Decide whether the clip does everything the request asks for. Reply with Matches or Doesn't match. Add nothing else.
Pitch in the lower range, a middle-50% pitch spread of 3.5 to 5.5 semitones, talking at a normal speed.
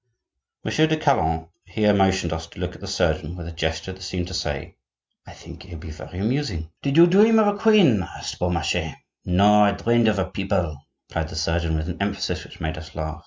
Doesn't match